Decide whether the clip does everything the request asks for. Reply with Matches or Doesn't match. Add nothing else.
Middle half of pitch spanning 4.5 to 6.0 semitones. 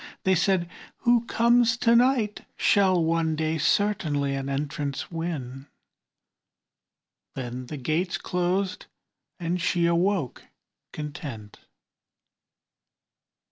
Matches